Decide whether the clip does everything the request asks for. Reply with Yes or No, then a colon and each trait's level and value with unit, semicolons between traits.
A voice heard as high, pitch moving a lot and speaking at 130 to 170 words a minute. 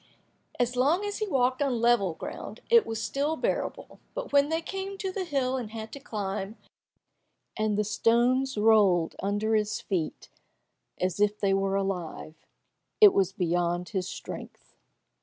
Yes: high, 220 Hz; wide, 5.9 semitones; average, 160 wpm